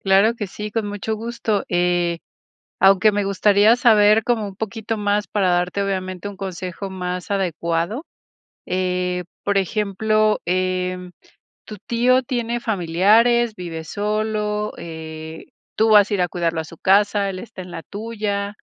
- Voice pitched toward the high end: Yes, high, 200 Hz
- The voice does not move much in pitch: No, average, 3.0 semitones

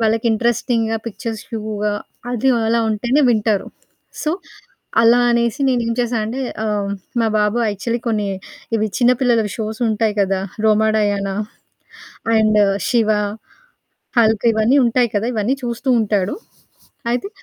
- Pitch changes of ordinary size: No, narrow, 2.0 semitones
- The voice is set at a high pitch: Yes, high, 225 Hz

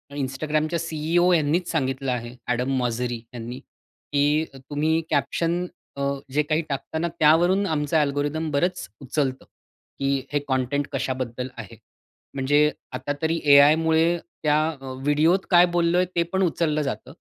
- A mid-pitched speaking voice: Yes, medium, 150 Hz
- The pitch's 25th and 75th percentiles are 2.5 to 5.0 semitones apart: Yes, average, 3.3 semitones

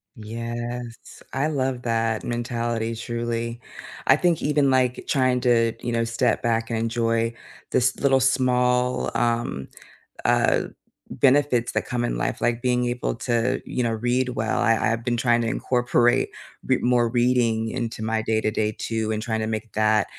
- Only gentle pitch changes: Yes, narrow, 1.5 semitones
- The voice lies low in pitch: Yes, low, 120 Hz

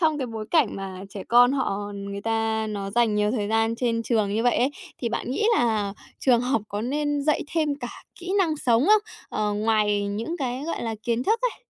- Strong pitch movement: No, average, 4.3 semitones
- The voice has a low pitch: No, high, 230 Hz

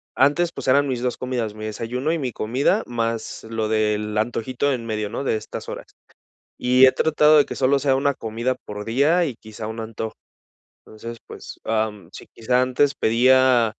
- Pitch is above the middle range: No, low, 120 Hz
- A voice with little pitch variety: No, average, 3.1 semitones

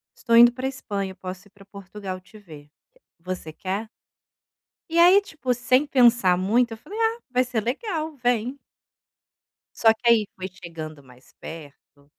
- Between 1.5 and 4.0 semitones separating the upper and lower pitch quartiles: No, wide, 5.4 semitones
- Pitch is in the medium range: No, high, 220 Hz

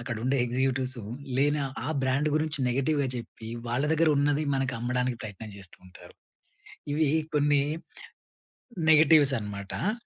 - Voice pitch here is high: No, low, 135 Hz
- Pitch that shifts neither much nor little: Yes, average, 3.6 semitones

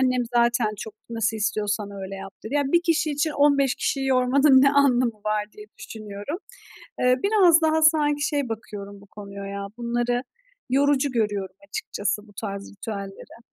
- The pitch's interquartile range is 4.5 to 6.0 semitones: Yes, wide, 5.5 semitones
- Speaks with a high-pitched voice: Yes, high, 240 Hz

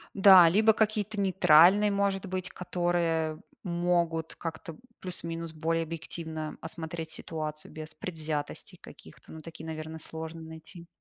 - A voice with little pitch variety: Yes, narrow, 2.3 semitones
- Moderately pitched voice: Yes, medium, 165 Hz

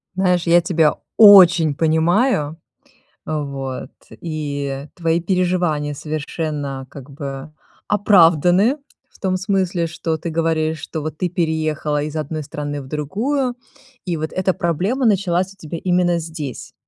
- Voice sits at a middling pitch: Yes, medium, 165 Hz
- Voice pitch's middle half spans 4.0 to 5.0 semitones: No, average, 3.2 semitones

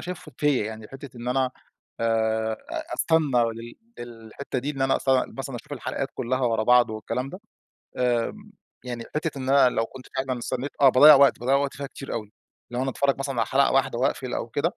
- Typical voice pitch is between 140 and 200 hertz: No, low, 130 Hz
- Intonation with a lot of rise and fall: No, average, 2.7 semitones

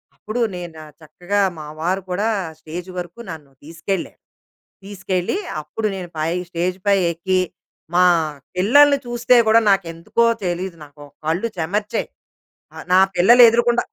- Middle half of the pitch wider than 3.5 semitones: Yes, average, 4.0 semitones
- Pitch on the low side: No, medium, 185 Hz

